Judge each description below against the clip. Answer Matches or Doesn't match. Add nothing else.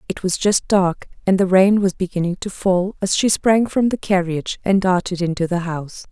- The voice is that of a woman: Matches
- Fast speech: Matches